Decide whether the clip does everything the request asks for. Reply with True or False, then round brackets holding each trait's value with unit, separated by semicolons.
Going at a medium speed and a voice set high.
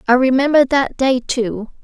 True (165 wpm; 255 Hz)